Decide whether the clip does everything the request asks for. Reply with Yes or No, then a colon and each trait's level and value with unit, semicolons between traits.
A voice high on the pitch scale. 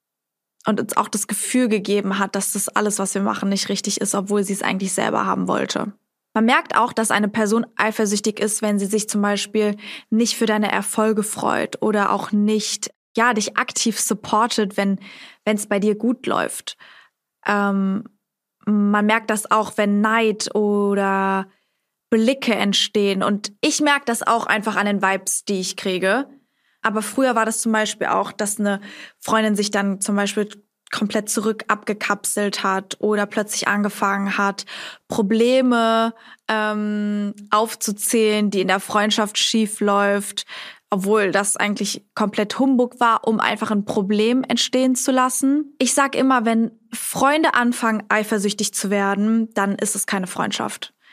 Yes: high, 210 Hz